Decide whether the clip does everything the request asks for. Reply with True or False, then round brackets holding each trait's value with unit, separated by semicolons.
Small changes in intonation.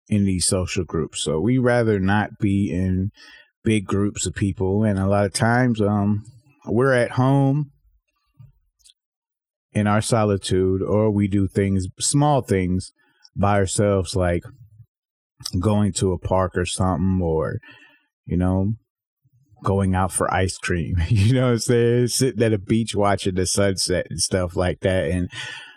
False (4.0 semitones)